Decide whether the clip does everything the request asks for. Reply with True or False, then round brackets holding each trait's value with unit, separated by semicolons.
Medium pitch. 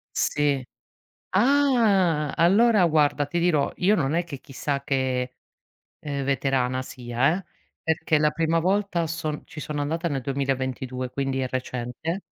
True (150 Hz)